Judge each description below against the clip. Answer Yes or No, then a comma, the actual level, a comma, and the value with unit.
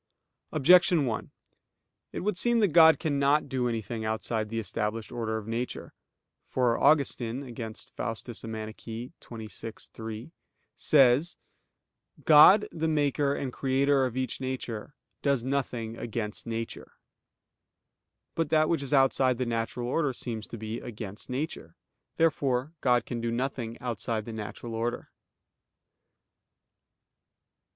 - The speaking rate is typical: No, slow, 125 wpm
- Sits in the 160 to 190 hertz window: No, low, 125 Hz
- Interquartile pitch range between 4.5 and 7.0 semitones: No, average, 3.7 semitones